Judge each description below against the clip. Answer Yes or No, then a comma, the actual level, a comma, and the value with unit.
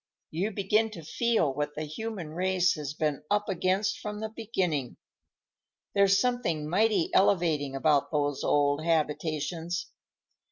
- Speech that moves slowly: Yes, slow, 130 wpm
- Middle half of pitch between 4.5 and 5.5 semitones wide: Yes, average, 5.0 semitones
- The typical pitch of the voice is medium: Yes, medium, 170 Hz